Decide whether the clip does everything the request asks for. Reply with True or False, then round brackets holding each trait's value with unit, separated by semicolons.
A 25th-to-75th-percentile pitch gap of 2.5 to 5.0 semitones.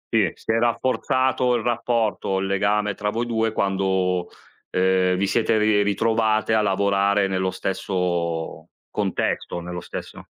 True (2.9 semitones)